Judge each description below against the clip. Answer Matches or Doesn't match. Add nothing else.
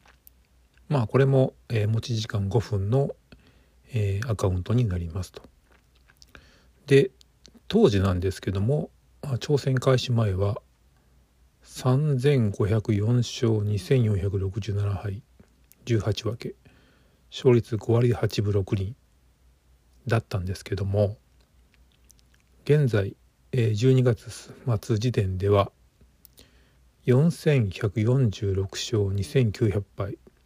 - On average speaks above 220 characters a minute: Doesn't match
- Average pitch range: Matches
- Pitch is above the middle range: Doesn't match